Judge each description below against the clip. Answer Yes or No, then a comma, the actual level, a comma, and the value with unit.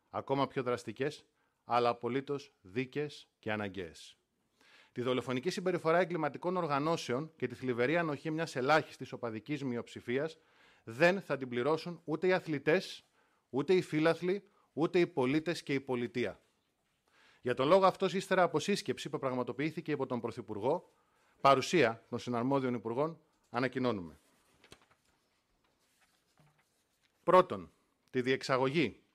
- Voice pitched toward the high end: No, low, 135 Hz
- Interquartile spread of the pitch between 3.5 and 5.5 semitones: Yes, average, 5.1 semitones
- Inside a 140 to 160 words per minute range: No, slow, 115 wpm